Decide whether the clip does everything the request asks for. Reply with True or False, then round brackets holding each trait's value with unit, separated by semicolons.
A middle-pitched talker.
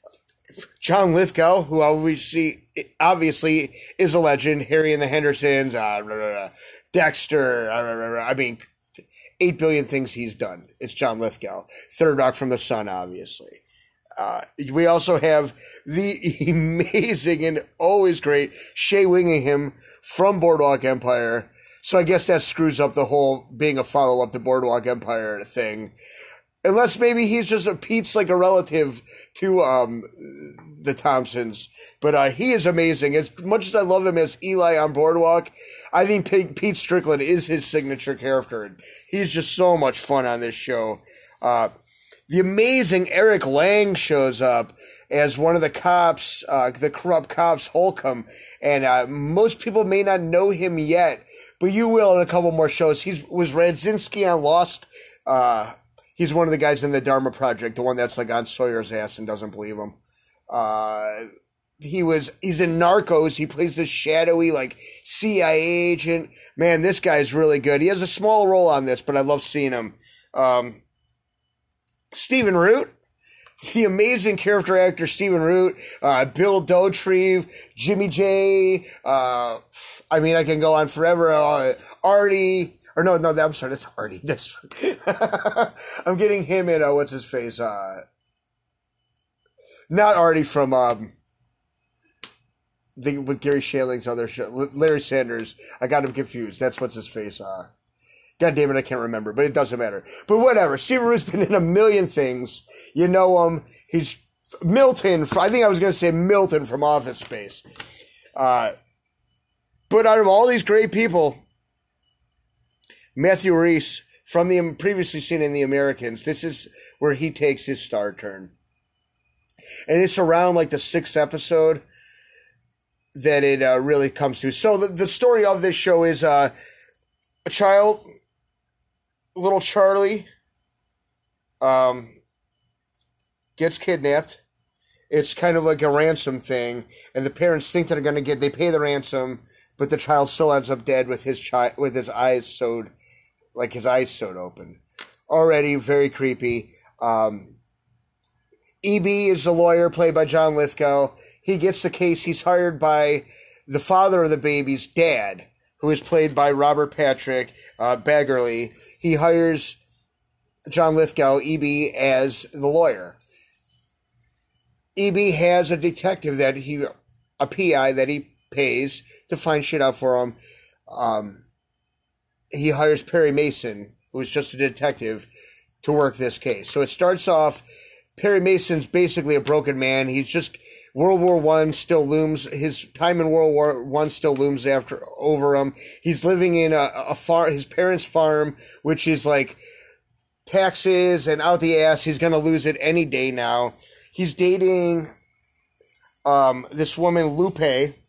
True (155 Hz)